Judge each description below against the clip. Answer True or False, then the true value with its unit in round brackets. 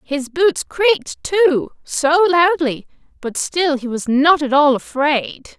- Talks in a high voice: True (305 Hz)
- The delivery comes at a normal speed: True (150 wpm)